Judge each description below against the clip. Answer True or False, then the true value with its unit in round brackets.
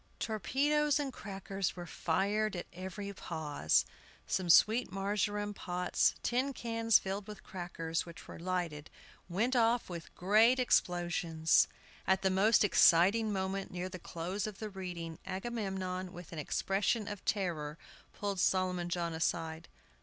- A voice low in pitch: False (190 Hz)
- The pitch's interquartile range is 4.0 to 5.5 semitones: False (3.4 semitones)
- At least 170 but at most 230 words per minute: False (140 wpm)